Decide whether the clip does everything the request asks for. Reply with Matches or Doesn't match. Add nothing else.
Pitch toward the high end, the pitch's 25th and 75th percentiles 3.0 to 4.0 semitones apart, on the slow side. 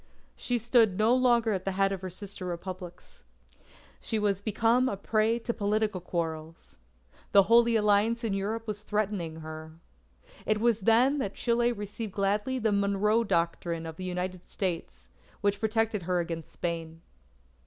Doesn't match